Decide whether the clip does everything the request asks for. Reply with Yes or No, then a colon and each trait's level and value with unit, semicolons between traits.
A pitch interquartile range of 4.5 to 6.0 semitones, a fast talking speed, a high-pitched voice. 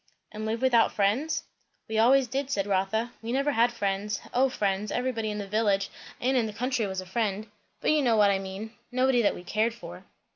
No: average, 3.7 semitones; fast, 215 wpm; high, 220 Hz